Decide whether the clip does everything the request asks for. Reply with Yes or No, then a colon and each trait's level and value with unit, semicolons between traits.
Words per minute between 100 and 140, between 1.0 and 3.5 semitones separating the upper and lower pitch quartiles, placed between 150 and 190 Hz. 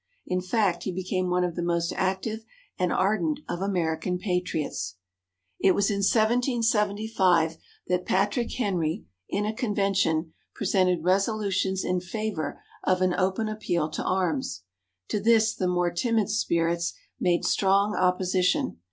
Yes: slow, 135 wpm; average, 2.9 semitones; medium, 185 Hz